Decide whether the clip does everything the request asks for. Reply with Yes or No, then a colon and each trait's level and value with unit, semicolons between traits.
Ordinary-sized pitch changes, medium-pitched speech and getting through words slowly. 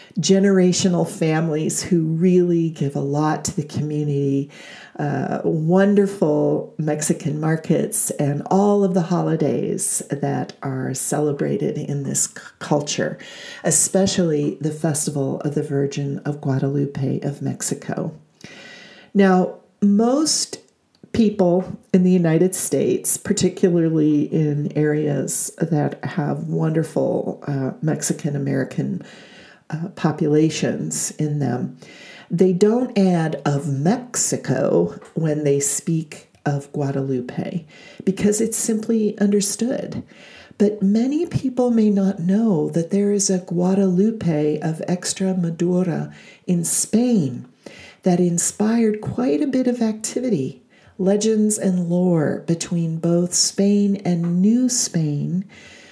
Yes: average, 4.7 semitones; medium, 175 Hz; slow, 110 wpm